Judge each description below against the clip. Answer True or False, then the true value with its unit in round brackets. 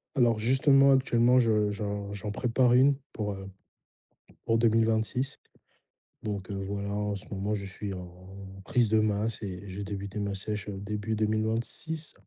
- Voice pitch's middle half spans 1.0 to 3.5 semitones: True (2.5 semitones)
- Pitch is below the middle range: True (105 Hz)